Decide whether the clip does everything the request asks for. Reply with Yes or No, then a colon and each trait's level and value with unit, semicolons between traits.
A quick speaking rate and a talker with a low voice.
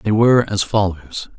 No: average, 175 wpm; low, 100 Hz